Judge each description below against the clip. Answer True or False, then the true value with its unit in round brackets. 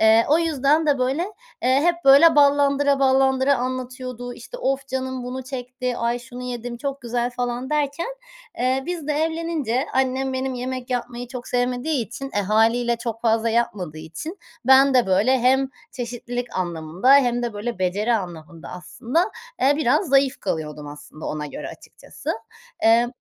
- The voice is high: True (250 Hz)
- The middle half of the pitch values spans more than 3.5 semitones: False (2.7 semitones)